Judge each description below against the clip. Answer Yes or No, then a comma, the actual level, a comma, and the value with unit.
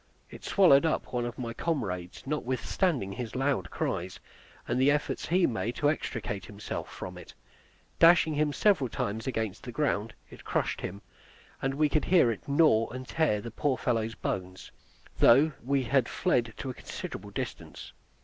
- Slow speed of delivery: No, average, 170 wpm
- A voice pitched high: No, low, 125 Hz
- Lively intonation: No, average, 4.7 semitones